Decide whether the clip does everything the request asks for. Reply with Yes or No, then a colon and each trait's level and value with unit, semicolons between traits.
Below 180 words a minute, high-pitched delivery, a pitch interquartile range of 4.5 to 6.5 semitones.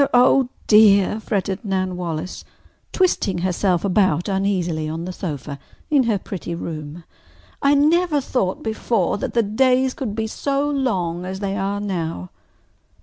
Yes: average, 145 wpm; high, 195 Hz; average, 5.2 semitones